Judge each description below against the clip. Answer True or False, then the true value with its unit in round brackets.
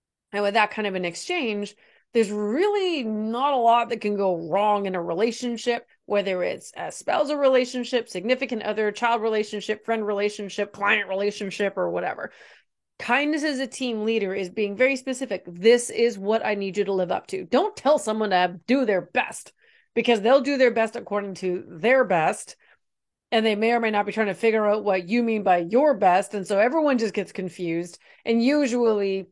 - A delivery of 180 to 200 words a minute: True (190 wpm)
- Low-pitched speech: False (220 Hz)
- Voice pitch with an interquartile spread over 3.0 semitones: True (3.5 semitones)